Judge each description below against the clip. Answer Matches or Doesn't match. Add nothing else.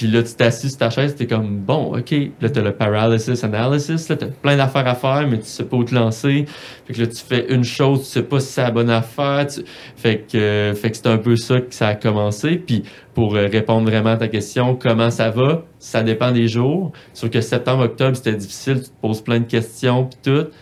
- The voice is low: Matches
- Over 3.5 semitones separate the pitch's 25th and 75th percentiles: Doesn't match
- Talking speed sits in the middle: Doesn't match